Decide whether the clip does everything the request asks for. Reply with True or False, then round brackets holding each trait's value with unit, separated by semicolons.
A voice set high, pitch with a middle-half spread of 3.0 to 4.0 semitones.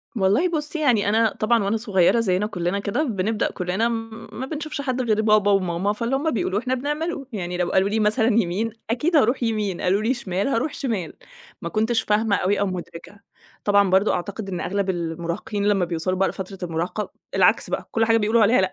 True (210 Hz; 3.6 semitones)